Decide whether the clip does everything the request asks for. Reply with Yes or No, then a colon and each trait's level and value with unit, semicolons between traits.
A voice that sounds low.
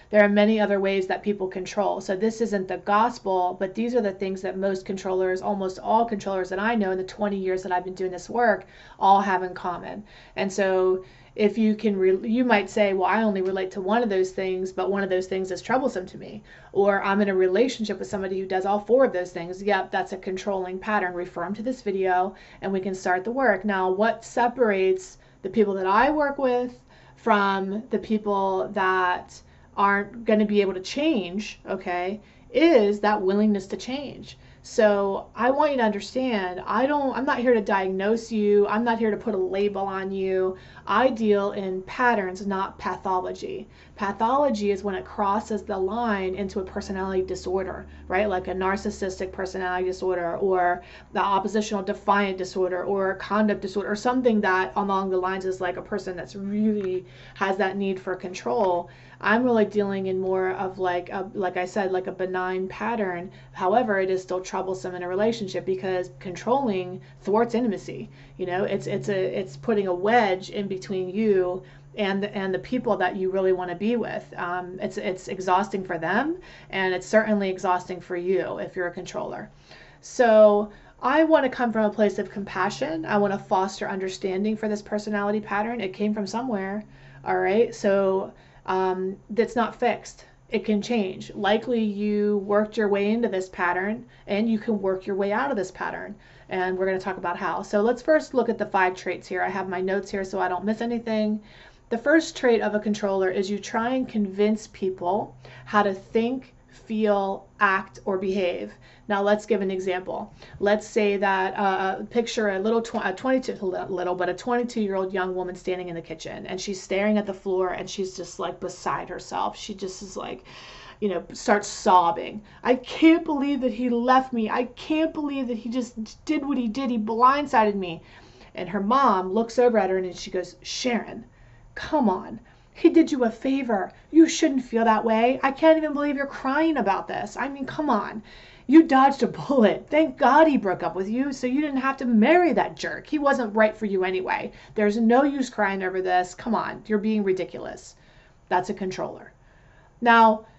No: high, 200 Hz